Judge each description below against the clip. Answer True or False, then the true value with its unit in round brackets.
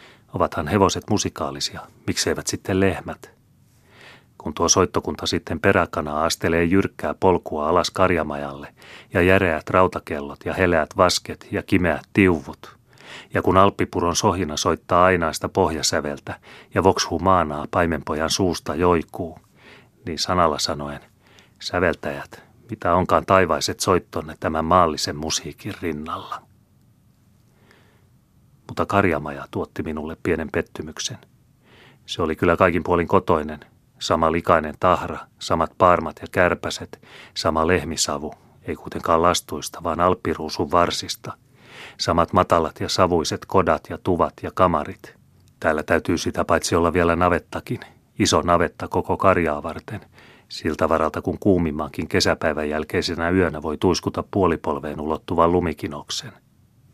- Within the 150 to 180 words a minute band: False (115 wpm)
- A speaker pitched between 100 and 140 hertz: False (90 Hz)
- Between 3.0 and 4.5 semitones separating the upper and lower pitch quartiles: True (3.5 semitones)